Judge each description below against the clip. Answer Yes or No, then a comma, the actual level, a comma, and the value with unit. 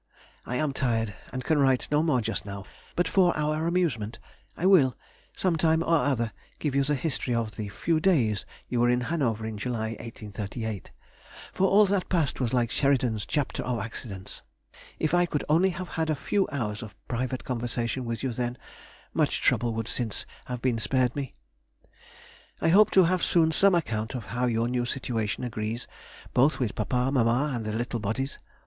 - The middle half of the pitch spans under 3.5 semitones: No, average, 5.2 semitones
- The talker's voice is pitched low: Yes, low, 125 Hz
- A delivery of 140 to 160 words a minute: No, average, 185 wpm